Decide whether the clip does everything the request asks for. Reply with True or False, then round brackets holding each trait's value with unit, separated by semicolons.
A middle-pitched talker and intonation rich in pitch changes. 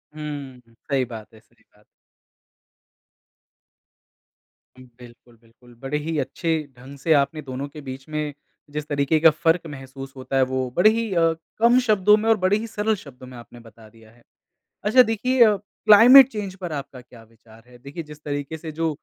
True (145 Hz; 6.5 semitones)